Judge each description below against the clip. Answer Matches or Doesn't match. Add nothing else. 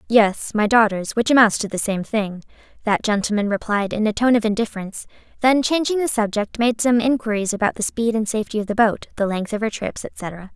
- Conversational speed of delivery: Doesn't match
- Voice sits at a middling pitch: Doesn't match